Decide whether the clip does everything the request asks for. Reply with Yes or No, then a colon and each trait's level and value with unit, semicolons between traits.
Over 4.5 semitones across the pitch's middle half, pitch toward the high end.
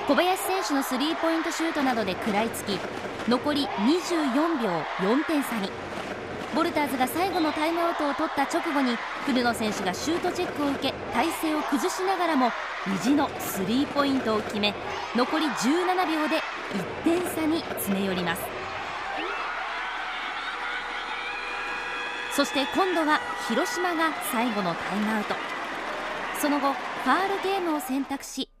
Yes: wide, 5.5 semitones; very high, 285 Hz